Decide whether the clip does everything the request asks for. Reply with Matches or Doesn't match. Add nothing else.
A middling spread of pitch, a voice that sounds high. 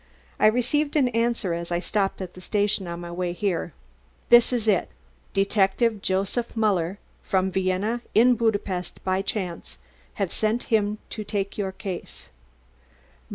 Matches